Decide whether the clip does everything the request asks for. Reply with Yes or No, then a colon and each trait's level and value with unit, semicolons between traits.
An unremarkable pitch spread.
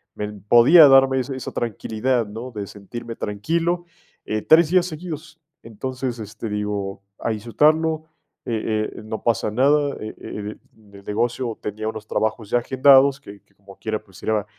Yes: average, 4.2 semitones